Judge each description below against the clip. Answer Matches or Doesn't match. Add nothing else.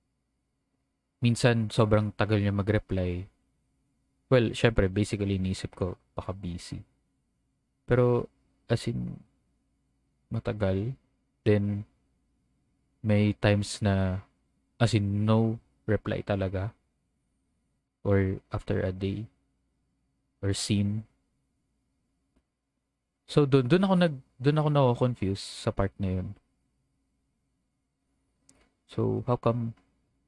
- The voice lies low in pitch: Matches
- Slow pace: Matches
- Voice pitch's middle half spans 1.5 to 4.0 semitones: Matches